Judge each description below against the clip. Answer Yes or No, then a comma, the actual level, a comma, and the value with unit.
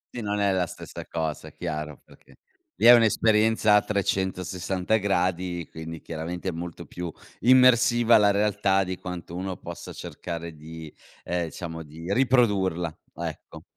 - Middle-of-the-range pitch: No, very low, 90 Hz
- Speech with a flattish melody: No, average, 3.8 semitones